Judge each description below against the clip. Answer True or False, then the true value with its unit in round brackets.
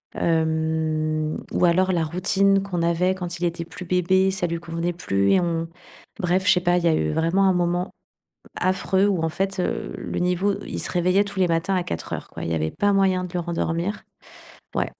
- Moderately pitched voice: True (175 Hz)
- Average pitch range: False (2.2 semitones)